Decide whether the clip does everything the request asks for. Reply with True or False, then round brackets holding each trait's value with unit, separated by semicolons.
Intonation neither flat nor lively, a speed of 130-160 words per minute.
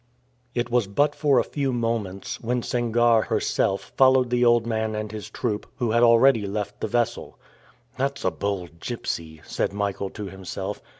False (3.3 semitones; 170 wpm)